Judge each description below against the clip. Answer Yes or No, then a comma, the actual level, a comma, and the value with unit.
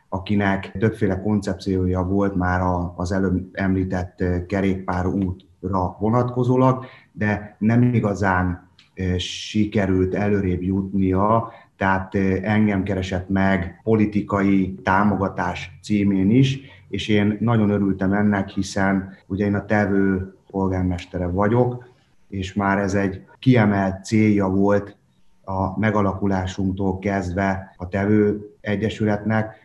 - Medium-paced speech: No, slow, 100 wpm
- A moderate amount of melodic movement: No, narrow, 1.7 semitones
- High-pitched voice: No, low, 100 Hz